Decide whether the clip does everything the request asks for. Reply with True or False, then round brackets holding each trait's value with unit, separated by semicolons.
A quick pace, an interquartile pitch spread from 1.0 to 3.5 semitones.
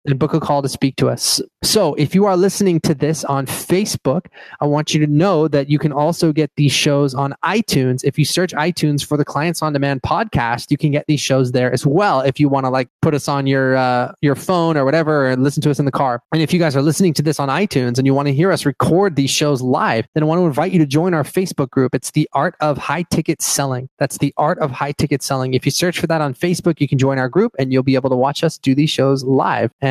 True (280 wpm; 3.0 semitones)